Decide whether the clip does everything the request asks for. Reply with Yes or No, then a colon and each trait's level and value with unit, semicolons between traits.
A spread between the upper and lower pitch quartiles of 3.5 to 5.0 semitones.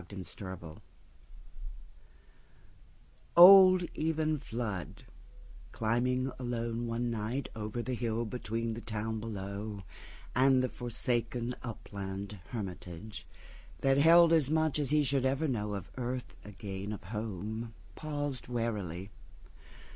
Yes: average, 4.0 semitones